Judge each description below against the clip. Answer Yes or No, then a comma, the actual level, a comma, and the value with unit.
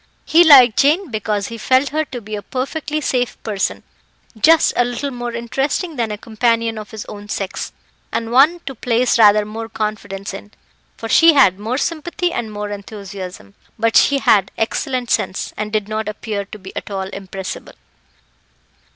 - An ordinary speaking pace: Yes, average, 175 wpm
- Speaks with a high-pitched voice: Yes, high, 225 Hz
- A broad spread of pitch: No, average, 4.1 semitones